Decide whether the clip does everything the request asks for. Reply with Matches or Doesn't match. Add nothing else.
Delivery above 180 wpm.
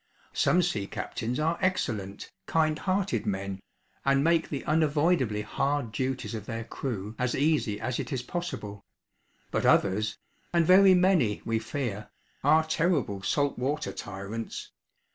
Doesn't match